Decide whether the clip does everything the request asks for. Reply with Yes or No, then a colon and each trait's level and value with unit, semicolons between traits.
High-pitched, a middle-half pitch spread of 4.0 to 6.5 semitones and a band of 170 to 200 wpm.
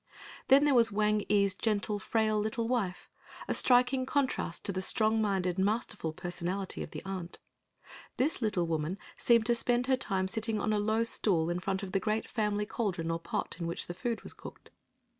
No: high, 210 Hz; average, 3.5 semitones; average, 195 wpm